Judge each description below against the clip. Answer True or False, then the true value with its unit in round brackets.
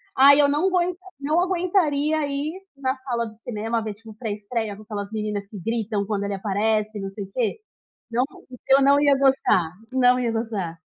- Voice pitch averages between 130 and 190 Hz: False (230 Hz)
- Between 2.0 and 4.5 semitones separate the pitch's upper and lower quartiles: False (5.1 semitones)